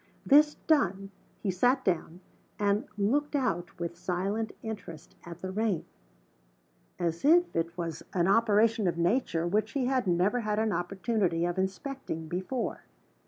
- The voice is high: Yes, high, 195 Hz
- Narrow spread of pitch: No, average, 4.9 semitones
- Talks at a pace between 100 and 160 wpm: Yes, average, 145 wpm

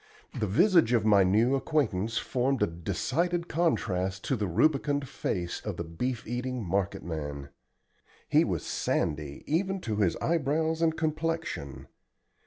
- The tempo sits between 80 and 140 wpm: Yes, slow, 135 wpm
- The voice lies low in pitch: Yes, low, 120 Hz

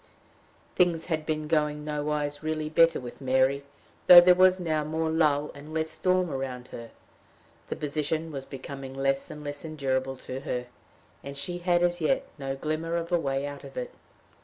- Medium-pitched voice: Yes, medium, 150 Hz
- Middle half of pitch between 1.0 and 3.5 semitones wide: Yes, average, 3.0 semitones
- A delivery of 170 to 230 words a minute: Yes, average, 180 wpm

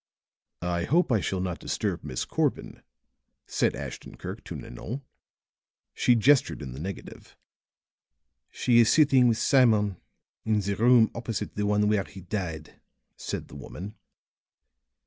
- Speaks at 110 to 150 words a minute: Yes, average, 140 wpm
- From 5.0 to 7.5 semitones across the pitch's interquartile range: No, average, 4.4 semitones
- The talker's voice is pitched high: No, low, 105 Hz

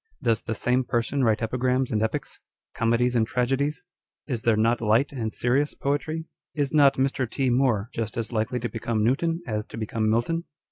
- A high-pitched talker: No, low, 120 Hz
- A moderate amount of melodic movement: Yes, average, 3.3 semitones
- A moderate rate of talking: Yes, average, 190 wpm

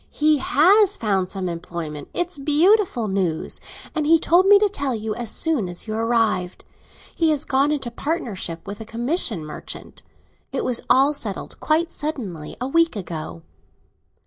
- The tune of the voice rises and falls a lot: Yes, wide, 8.5 semitones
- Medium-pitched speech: No, high, 245 Hz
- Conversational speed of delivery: Yes, average, 160 wpm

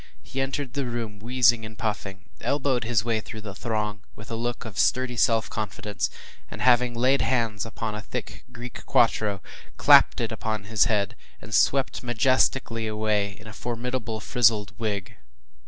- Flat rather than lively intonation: Yes, narrow, 2.3 semitones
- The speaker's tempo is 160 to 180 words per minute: Yes, average, 165 wpm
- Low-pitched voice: Yes, low, 115 Hz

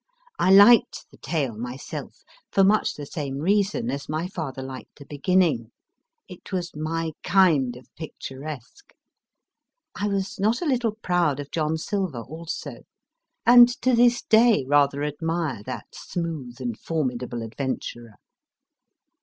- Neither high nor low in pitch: Yes, medium, 160 Hz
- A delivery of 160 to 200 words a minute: No, slow, 135 wpm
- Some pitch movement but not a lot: No, wide, 6.3 semitones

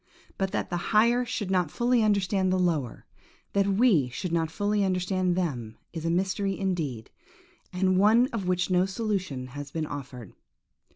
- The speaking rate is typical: Yes, average, 165 wpm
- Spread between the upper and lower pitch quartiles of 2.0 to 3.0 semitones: No, average, 3.6 semitones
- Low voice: No, medium, 185 Hz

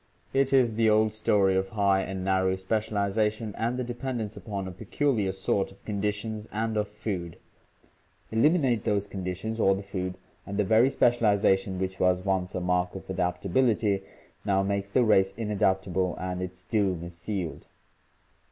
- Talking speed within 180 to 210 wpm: No, average, 165 wpm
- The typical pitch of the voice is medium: No, low, 100 Hz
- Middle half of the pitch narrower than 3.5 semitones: Yes, average, 2.7 semitones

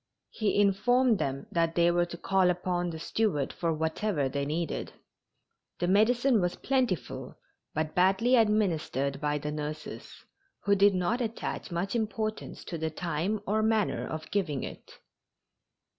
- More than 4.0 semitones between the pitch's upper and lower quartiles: Yes, average, 5.2 semitones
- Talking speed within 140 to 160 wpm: Yes, average, 145 wpm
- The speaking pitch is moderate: Yes, medium, 180 Hz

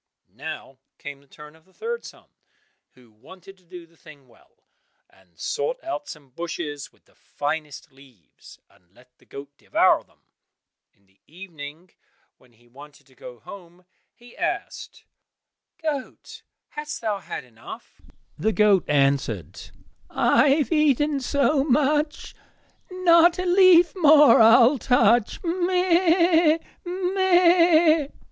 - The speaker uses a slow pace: Yes, slow, 130 wpm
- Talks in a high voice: Yes, high, 225 Hz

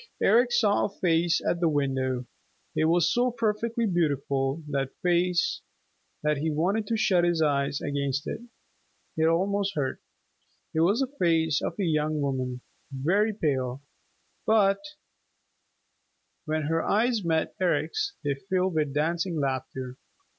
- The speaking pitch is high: No, medium, 165 Hz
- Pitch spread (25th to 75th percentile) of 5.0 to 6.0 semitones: Yes, wide, 5.6 semitones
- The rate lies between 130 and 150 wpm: Yes, average, 140 wpm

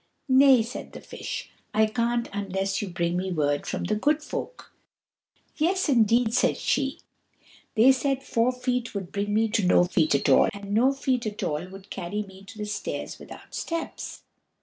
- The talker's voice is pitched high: Yes, high, 215 Hz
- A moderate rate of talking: Yes, average, 180 wpm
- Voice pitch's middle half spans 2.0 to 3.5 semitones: No, average, 4.7 semitones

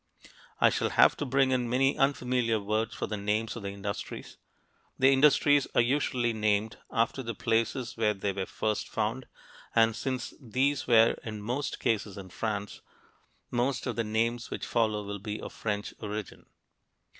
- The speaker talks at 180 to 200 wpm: No, average, 165 wpm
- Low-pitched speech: Yes, low, 115 Hz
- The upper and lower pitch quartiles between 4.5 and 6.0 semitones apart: No, average, 3.2 semitones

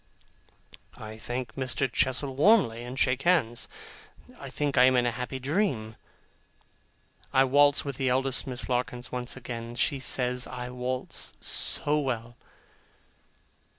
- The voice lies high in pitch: No, low, 130 Hz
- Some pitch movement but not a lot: No, narrow, 1.8 semitones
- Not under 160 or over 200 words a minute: No, slow, 135 wpm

